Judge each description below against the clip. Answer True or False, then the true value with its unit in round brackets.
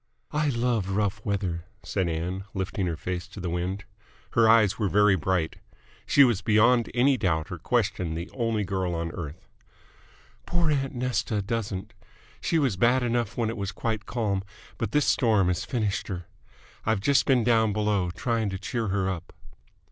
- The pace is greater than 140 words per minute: True (175 wpm)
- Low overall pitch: True (105 Hz)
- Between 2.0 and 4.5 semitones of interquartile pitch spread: True (4.1 semitones)